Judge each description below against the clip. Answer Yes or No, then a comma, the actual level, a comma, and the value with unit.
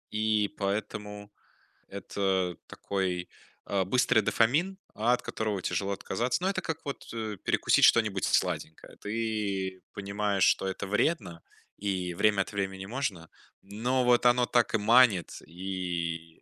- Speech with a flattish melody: No, average, 3.2 semitones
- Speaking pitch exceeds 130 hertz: No, low, 100 Hz